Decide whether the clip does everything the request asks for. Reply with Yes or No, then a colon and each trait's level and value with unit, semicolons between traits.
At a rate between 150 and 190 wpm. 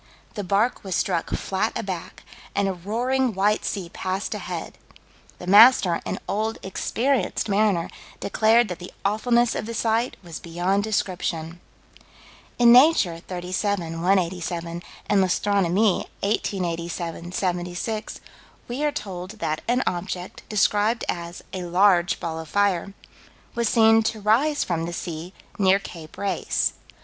No: slow, 135 wpm